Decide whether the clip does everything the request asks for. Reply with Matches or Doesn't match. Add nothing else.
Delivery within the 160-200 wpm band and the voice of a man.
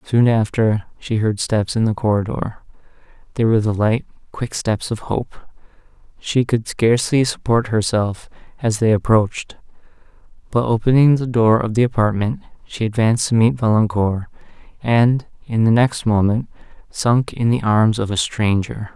Doesn't match